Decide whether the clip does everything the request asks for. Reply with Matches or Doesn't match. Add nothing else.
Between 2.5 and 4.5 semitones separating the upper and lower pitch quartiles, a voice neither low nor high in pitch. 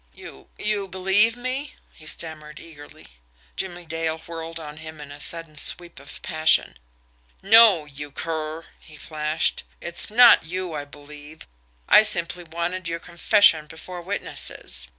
Matches